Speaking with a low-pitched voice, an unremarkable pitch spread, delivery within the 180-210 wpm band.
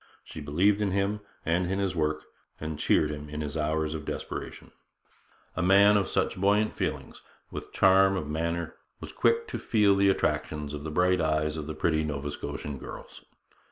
Yes: very low, 80 Hz; average, 4.3 semitones; average, 190 wpm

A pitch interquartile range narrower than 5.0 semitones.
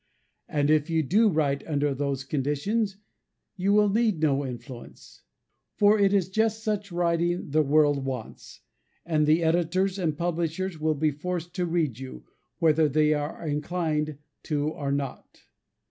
Yes: average, 3.7 semitones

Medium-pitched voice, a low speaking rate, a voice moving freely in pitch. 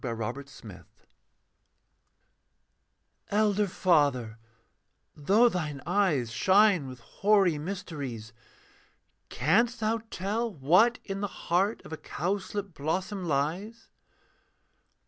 Yes: medium, 180 Hz; slow, 100 wpm; wide, 6.3 semitones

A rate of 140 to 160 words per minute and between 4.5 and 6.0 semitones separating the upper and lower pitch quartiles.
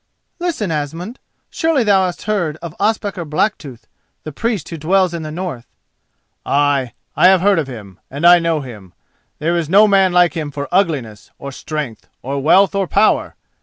No: average, 170 wpm; average, 5.3 semitones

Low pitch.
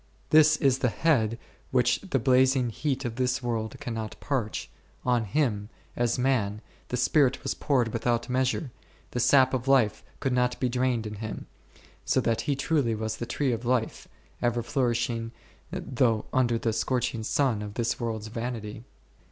Yes: low, 120 Hz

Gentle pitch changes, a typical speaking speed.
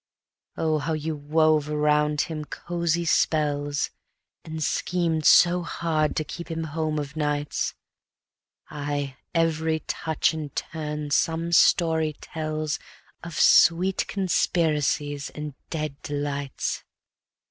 No: narrow, 1.7 semitones; slow, 110 wpm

